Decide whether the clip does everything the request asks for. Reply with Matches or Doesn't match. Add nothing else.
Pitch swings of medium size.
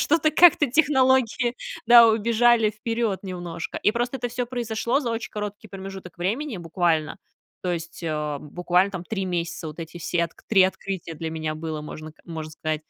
Doesn't match